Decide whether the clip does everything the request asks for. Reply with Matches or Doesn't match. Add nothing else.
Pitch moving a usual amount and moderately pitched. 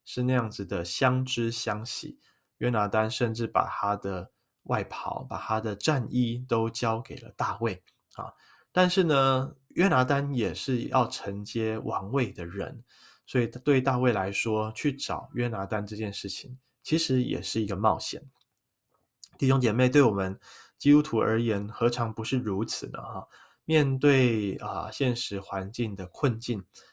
Doesn't match